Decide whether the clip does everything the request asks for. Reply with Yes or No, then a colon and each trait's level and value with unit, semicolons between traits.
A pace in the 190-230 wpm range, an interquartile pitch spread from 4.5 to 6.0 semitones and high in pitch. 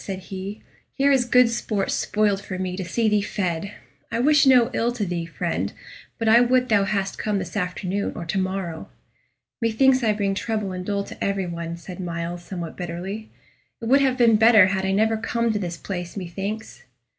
No: average, 200 wpm; average, 3.7 semitones; high, 200 Hz